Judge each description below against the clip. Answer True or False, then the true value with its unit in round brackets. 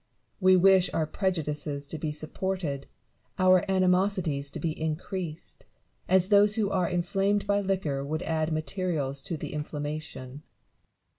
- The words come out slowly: False (145 wpm)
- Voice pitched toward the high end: False (170 Hz)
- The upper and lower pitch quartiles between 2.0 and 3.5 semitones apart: False (3.9 semitones)